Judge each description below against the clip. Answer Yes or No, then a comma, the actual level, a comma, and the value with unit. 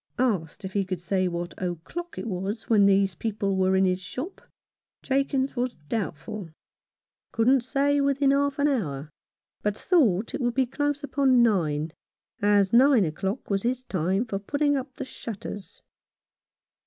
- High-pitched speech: Yes, high, 215 Hz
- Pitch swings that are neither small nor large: No, wide, 6.1 semitones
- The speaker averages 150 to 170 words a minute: Yes, average, 160 wpm